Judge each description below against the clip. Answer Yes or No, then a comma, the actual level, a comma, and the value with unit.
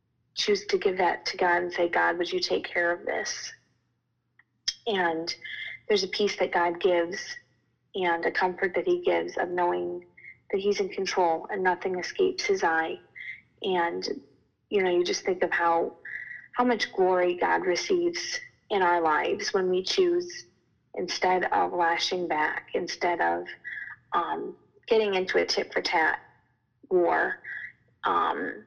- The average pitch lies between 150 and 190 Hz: Yes, medium, 185 Hz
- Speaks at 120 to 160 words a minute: Yes, average, 155 wpm